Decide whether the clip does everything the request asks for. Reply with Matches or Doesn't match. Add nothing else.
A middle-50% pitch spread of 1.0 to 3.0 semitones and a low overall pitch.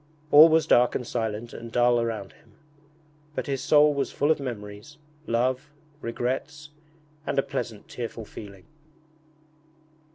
Doesn't match